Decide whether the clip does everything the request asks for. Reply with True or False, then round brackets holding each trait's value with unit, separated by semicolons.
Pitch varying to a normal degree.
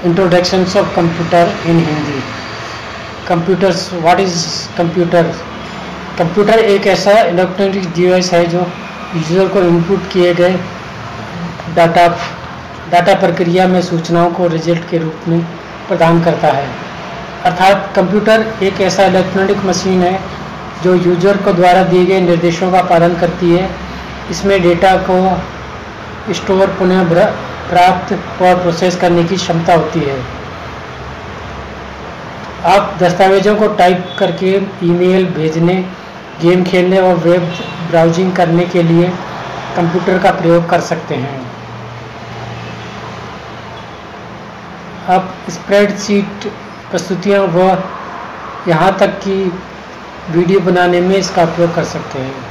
False (1.7 semitones)